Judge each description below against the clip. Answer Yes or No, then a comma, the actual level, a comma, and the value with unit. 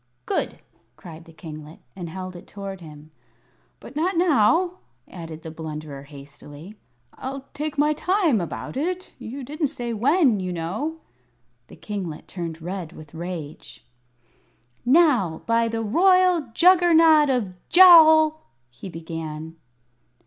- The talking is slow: Yes, slow, 130 wpm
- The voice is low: No, high, 210 Hz